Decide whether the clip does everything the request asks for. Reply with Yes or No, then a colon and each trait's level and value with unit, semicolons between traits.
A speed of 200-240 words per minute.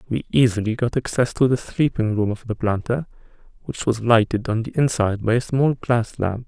Yes: fast, 205 wpm